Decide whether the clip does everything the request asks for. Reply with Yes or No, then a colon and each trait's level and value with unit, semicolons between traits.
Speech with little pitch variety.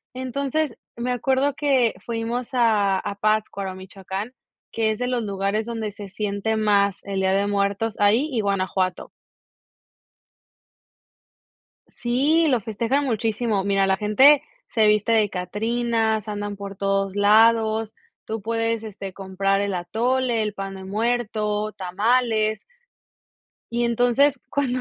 No: average, 3.1 semitones